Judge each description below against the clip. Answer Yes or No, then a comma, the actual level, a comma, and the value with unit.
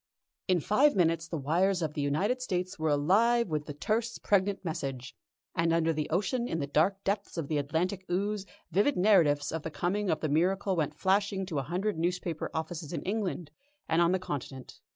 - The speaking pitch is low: No, medium, 175 Hz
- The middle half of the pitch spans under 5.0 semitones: Yes, average, 4.1 semitones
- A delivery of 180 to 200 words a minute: Yes, average, 195 wpm